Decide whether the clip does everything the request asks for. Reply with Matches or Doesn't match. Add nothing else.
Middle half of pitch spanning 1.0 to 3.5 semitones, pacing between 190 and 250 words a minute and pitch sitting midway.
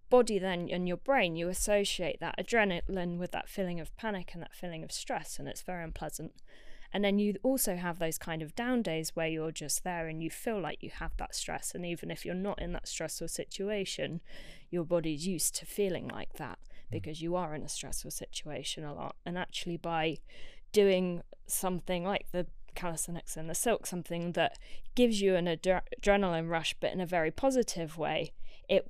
Matches